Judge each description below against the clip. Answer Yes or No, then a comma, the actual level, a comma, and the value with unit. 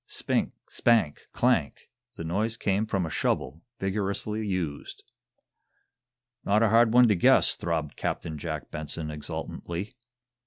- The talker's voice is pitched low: Yes, very low, 95 Hz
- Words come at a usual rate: No, slow, 125 wpm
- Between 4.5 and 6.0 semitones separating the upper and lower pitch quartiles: Yes, average, 5.2 semitones